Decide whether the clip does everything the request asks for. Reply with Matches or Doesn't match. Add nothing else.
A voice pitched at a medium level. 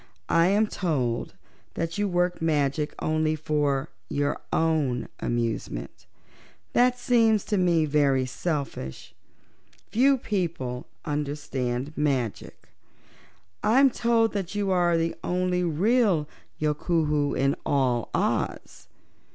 Matches